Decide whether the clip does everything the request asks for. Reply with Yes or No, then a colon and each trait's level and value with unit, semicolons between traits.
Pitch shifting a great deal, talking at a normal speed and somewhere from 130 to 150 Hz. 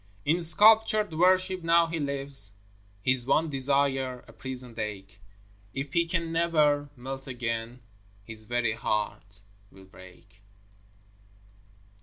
No: wide, 6.5 semitones; slow, 115 wpm; low, 135 Hz